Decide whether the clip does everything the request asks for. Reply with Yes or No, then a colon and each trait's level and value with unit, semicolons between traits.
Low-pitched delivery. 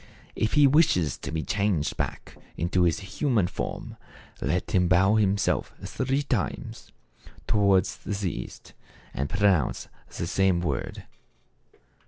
Yes: very low, 95 Hz